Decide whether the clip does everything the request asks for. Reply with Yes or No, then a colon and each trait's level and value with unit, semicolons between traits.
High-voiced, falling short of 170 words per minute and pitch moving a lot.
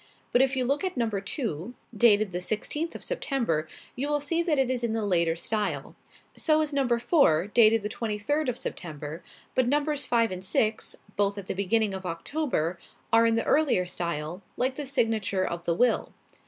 No: high, 225 Hz; average, 195 wpm; wide, 6.4 semitones